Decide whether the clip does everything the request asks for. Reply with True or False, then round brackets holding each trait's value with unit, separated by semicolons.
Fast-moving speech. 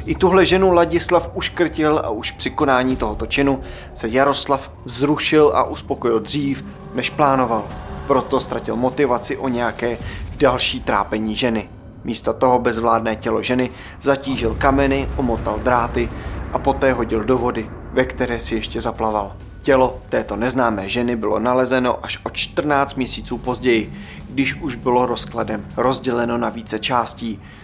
False (140 wpm)